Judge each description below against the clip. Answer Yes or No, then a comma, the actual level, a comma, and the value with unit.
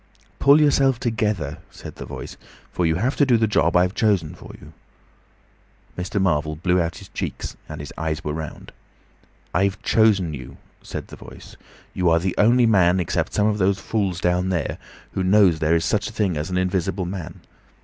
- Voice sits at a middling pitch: No, very low, 90 Hz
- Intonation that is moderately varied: Yes, average, 4.3 semitones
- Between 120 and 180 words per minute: No, average, 190 wpm